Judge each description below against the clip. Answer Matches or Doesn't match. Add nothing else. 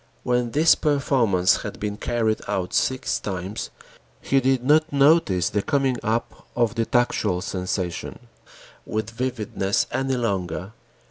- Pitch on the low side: Matches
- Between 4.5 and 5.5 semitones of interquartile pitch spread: Matches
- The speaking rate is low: Matches